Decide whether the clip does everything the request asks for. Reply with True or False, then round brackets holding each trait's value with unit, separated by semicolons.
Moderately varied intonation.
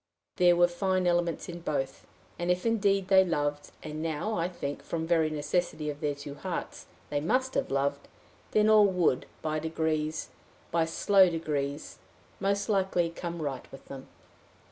True (3.7 semitones)